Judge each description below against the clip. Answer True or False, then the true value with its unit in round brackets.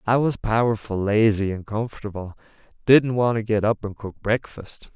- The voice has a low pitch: True (110 Hz)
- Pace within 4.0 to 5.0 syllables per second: True (4.9 syllables/s)